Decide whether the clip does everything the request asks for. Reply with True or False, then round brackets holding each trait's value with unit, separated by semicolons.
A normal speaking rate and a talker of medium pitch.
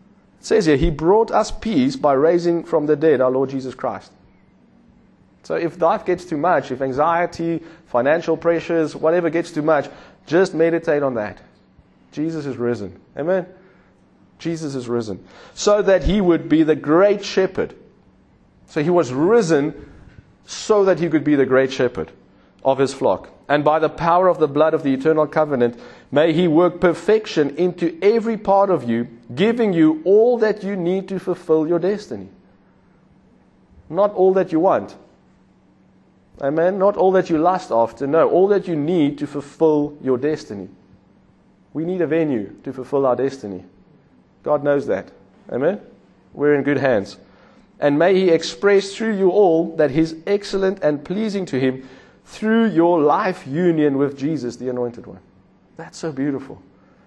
True (165 wpm; 160 Hz)